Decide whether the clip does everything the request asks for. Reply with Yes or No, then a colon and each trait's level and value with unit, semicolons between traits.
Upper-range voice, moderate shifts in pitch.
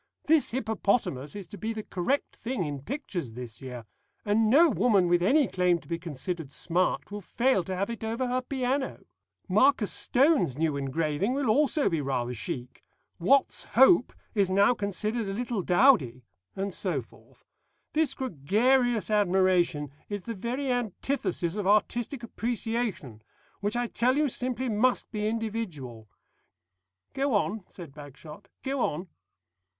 No: high, 205 Hz; wide, 6.5 semitones